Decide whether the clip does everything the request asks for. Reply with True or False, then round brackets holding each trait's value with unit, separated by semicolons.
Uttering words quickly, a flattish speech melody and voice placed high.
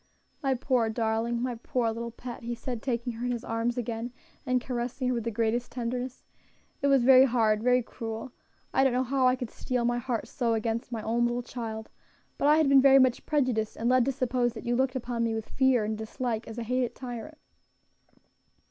True (215 wpm; 1.8 semitones; 240 Hz)